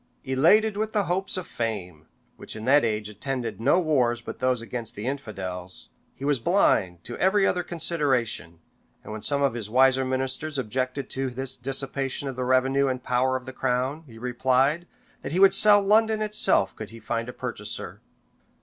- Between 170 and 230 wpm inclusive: Yes, average, 185 wpm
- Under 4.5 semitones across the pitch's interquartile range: Yes, average, 4.1 semitones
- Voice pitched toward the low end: Yes, low, 130 Hz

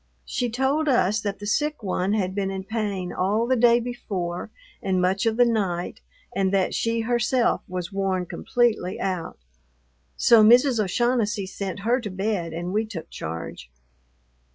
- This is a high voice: Yes, high, 205 Hz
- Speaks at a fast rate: No, average, 160 wpm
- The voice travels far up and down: No, average, 4.0 semitones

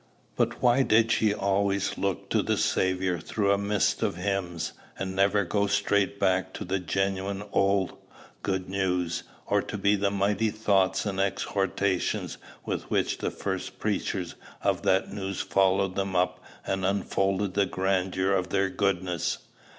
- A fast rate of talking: No, average, 150 wpm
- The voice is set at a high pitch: No, very low, 95 Hz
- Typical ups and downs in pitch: No, narrow, 1.2 semitones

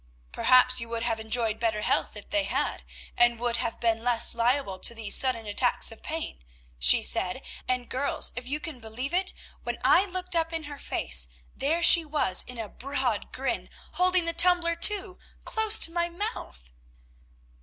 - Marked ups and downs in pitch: Yes, wide, 6.7 semitones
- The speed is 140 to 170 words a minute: No, average, 180 wpm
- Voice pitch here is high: Yes, very high, 255 Hz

